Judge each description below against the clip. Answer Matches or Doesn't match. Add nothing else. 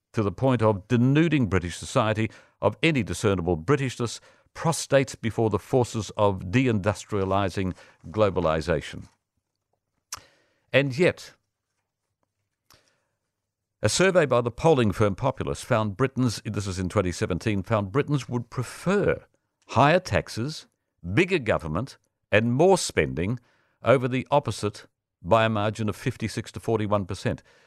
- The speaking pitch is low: Matches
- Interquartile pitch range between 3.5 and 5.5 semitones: Matches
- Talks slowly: Matches